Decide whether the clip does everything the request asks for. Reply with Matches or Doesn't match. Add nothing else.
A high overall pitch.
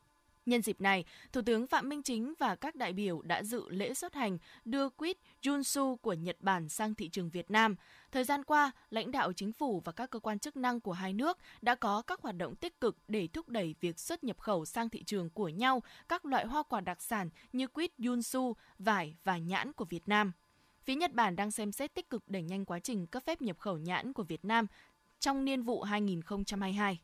Matches